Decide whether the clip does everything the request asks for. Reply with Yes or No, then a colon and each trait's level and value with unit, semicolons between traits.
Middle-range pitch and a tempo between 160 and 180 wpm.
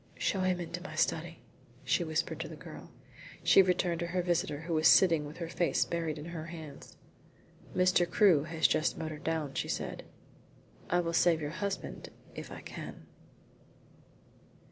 Yes: medium, 170 Hz; average, 165 wpm